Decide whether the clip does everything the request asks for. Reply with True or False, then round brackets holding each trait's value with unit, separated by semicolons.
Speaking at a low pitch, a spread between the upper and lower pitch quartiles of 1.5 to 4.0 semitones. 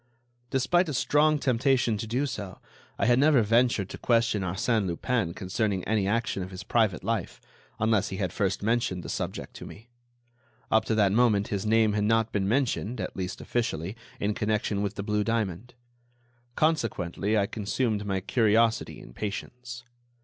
True (110 Hz; 3.3 semitones)